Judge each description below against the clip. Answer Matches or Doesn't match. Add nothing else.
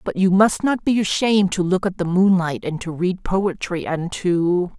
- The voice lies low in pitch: Doesn't match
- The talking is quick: Matches